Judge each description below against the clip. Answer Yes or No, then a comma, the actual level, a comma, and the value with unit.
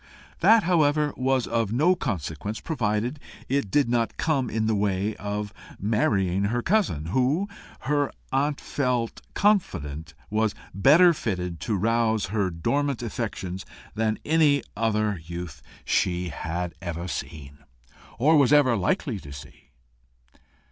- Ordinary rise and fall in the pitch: No, wide, 7.2 semitones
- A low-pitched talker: Yes, low, 110 Hz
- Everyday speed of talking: No, slow, 130 wpm